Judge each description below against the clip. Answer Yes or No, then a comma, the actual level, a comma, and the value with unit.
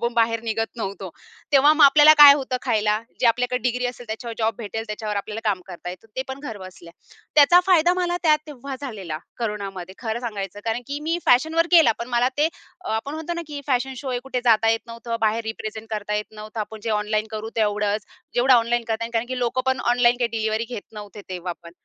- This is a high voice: Yes, high, 230 Hz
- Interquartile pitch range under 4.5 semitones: Yes, average, 3.5 semitones